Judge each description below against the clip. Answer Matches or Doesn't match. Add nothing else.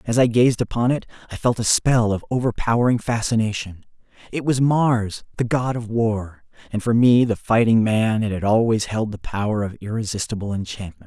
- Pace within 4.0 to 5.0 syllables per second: Doesn't match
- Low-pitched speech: Matches